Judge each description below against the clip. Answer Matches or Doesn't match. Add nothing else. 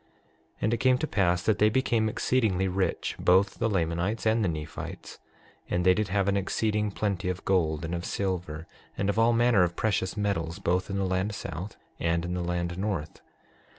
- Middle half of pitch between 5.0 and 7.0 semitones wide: Doesn't match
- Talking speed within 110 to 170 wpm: Doesn't match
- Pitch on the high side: Doesn't match